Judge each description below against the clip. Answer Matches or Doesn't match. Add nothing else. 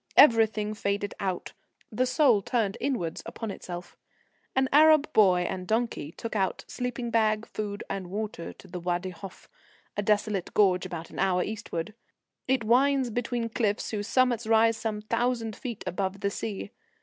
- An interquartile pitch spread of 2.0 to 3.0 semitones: Doesn't match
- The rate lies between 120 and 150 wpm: Doesn't match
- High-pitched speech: Matches